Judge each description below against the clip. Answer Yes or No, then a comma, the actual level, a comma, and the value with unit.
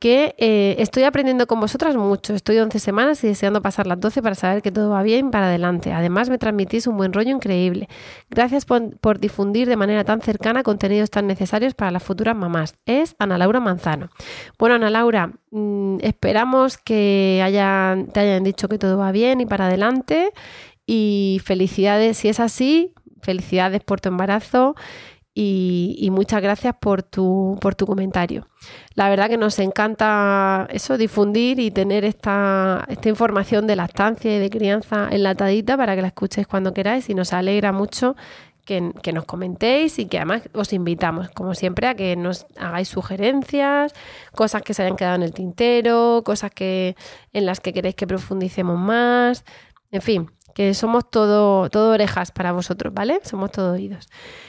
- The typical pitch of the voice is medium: No, high, 205 Hz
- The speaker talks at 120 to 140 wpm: No, average, 175 wpm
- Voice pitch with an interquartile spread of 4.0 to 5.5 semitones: No, average, 2.9 semitones